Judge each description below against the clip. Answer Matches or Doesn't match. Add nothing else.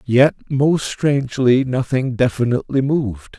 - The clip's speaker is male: Matches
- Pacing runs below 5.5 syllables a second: Matches